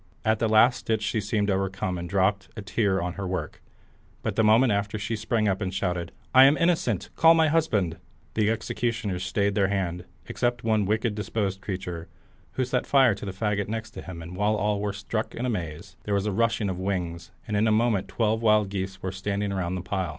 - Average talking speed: No, fast, 220 wpm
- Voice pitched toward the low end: Yes, low, 105 Hz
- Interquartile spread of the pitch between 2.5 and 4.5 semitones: Yes, average, 2.8 semitones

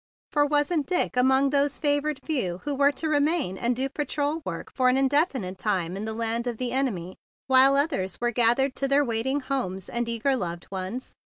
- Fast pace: Yes, fast, 210 wpm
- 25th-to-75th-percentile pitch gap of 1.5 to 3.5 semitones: No, average, 4.2 semitones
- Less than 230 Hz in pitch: No, very high, 260 Hz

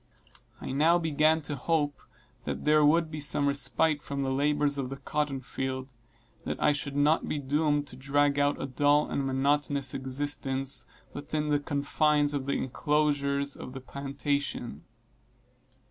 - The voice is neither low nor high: Yes, medium, 145 Hz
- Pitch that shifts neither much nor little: No, narrow, 1.4 semitones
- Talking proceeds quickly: No, average, 160 wpm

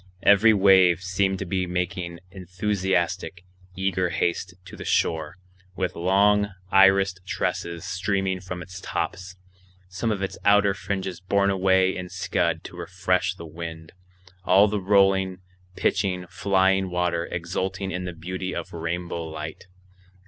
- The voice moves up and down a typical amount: No, narrow, 1.5 semitones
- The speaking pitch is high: No, very low, 95 Hz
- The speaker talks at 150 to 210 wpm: No, slow, 135 wpm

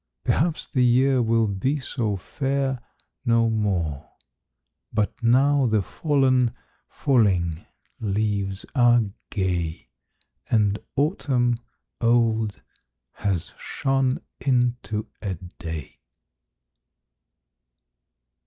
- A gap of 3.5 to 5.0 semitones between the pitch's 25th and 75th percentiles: Yes, average, 4.5 semitones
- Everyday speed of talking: No, slow, 80 wpm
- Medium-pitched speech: No, low, 115 Hz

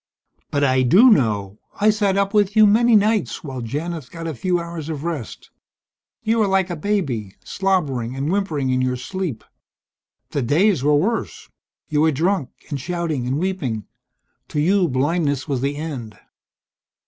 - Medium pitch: Yes, medium, 160 Hz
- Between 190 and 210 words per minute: No, average, 165 wpm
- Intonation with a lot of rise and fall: Yes, wide, 6.5 semitones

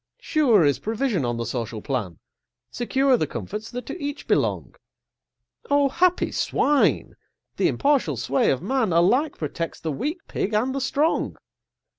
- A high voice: Yes, high, 230 Hz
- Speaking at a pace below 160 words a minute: Yes, average, 150 wpm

